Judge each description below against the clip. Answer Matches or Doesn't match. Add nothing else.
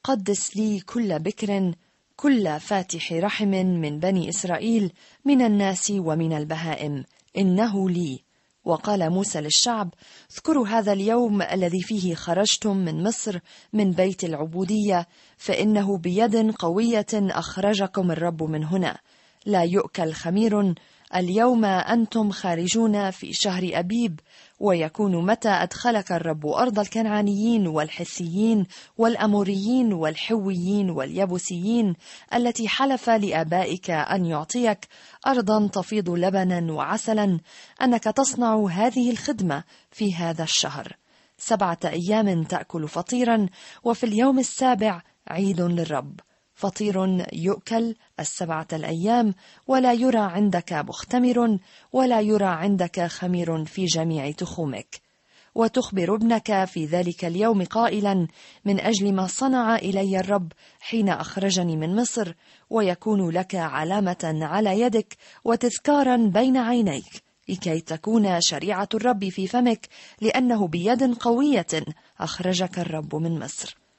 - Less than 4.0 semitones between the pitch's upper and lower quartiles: Doesn't match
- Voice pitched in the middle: Doesn't match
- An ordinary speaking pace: Matches